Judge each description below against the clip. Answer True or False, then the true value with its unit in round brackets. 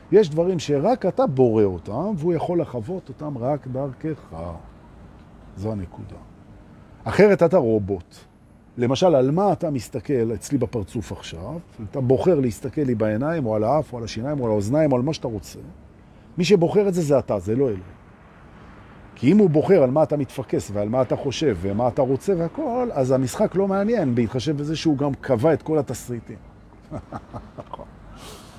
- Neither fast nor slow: False (170 wpm)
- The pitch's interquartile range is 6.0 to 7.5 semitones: True (6.8 semitones)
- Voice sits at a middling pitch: False (130 Hz)